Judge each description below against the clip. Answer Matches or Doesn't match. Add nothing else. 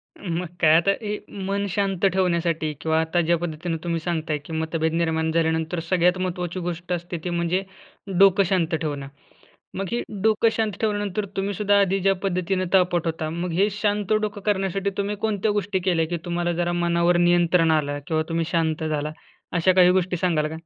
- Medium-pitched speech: Matches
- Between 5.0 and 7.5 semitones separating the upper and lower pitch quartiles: Doesn't match